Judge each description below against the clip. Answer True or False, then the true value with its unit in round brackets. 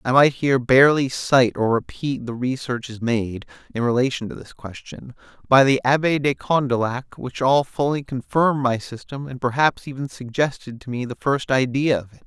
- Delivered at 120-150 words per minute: False (180 wpm)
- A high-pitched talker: False (130 Hz)